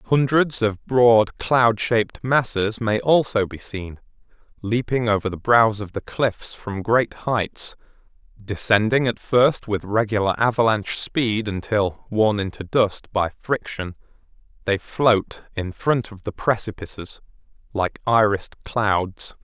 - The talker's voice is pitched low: Yes, low, 110 Hz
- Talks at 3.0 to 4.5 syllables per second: Yes, 3.9 syllables/s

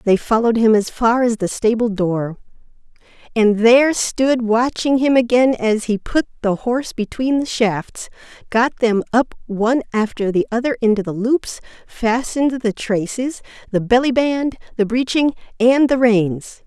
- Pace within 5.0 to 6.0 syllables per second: No, 4.5 syllables/s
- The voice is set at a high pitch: Yes, high, 235 Hz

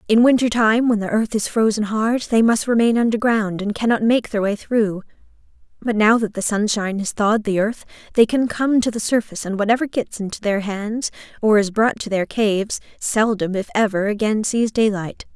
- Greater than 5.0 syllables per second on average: Yes, 5.3 syllables/s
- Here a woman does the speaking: Yes, female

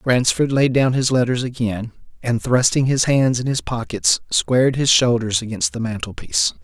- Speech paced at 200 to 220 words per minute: No, average, 170 wpm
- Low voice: Yes, low, 120 Hz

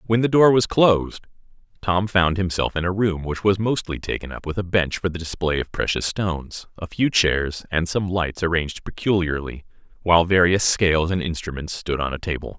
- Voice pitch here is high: No, very low, 90 Hz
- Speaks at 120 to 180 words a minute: No, average, 200 wpm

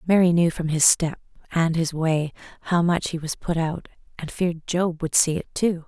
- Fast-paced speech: Yes, fast, 215 wpm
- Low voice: No, medium, 165 Hz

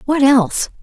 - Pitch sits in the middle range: No, very high, 260 Hz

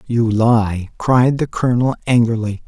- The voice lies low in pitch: Yes, low, 115 Hz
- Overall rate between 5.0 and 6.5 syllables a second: No, 4.3 syllables/s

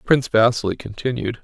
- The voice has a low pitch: Yes, low, 115 Hz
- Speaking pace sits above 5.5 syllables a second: Yes, 6.0 syllables/s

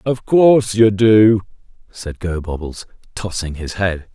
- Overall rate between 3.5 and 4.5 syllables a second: Yes, 4.0 syllables/s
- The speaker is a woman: No, male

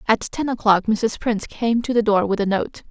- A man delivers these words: No, female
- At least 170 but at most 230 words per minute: No, fast, 250 wpm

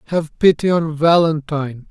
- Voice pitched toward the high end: No, medium, 155 Hz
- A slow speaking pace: Yes, slow, 125 wpm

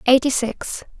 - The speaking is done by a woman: Yes, female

